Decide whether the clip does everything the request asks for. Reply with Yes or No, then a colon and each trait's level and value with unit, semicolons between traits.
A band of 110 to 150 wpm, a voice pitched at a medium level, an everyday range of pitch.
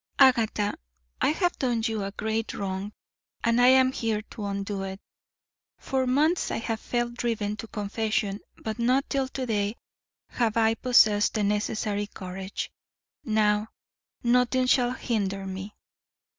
No: average, 145 wpm; high, 220 Hz; average, 3.1 semitones